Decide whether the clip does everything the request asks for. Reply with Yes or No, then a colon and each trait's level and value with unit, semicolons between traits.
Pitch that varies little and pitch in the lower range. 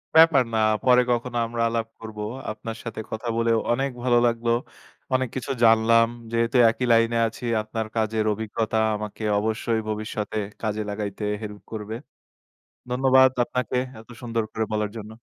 Yes: narrow, 1.7 semitones; low, 115 Hz